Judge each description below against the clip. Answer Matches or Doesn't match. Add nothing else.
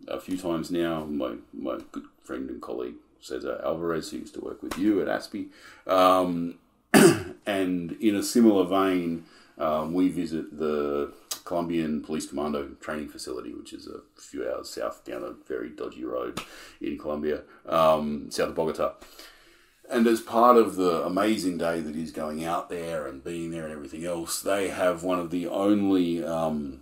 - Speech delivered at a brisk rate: Doesn't match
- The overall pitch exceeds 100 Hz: Doesn't match